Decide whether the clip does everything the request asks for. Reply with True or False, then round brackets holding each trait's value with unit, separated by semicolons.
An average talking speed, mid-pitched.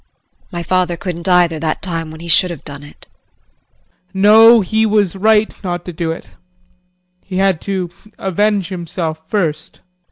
True (160 wpm; 180 Hz)